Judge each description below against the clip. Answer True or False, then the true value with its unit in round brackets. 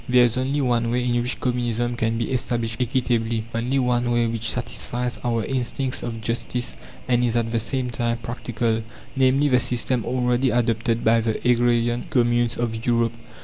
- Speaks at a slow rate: False (175 wpm)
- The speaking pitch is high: False (120 Hz)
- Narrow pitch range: True (1.2 semitones)